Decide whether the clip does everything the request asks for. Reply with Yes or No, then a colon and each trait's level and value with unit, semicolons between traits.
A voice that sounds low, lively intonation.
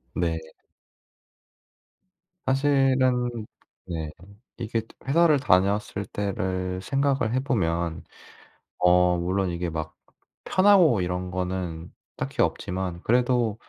Yes: very low, 95 Hz; wide, 6.3 semitones